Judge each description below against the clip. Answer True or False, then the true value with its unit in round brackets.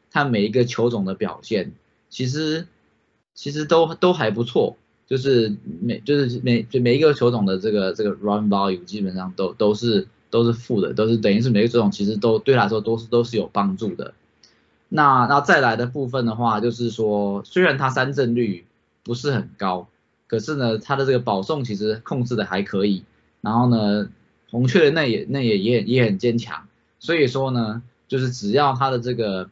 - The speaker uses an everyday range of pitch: True (3.8 semitones)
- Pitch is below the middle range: True (115 Hz)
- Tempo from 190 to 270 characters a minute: False (285 characters per minute)